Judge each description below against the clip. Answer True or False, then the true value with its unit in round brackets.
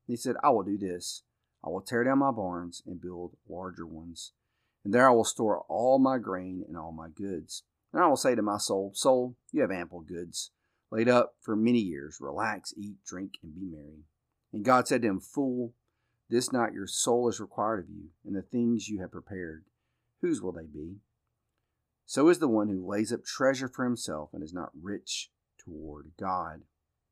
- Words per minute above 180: True (200 wpm)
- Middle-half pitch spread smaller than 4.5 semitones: False (5.2 semitones)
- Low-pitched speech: True (100 Hz)